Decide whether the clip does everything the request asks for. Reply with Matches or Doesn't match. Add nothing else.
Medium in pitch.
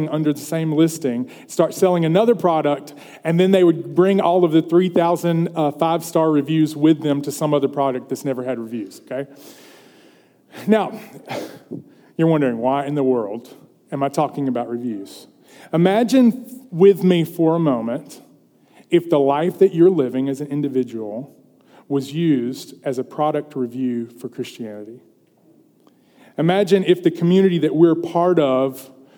Matches